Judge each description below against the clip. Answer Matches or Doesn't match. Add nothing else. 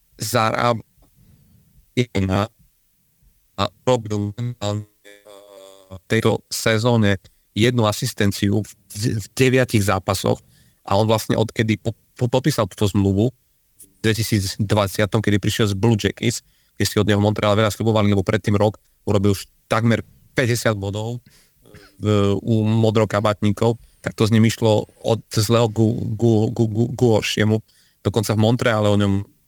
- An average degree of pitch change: Doesn't match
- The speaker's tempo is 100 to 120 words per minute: Matches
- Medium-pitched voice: Doesn't match